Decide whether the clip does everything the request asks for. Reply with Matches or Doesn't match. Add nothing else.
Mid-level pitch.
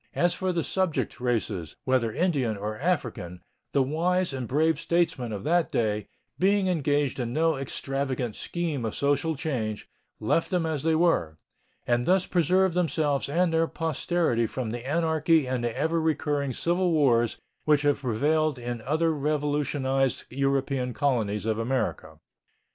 Matches